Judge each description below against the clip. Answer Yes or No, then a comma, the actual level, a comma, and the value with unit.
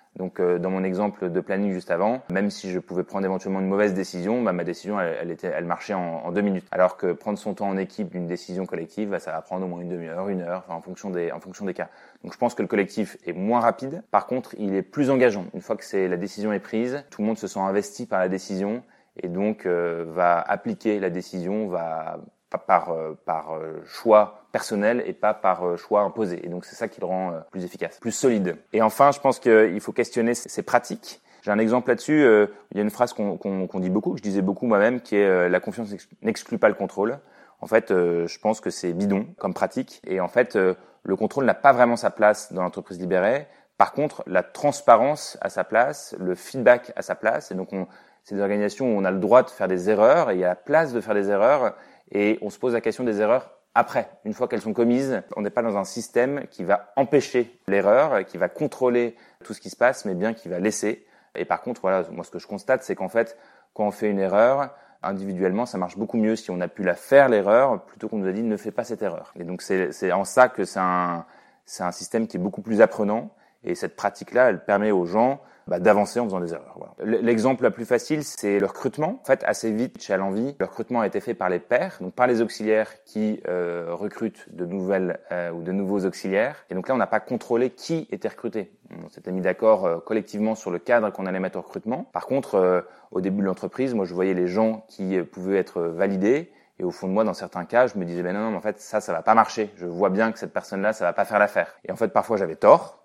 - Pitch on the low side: Yes, low, 100 Hz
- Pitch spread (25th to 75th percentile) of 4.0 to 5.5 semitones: No, average, 3.3 semitones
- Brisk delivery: Yes, fast, 255 wpm